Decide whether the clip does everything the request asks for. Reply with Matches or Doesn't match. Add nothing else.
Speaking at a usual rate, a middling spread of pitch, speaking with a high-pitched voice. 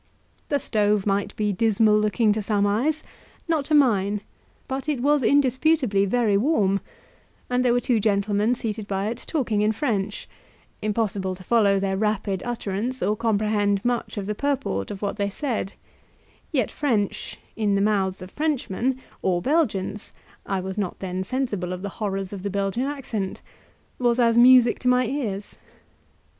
Matches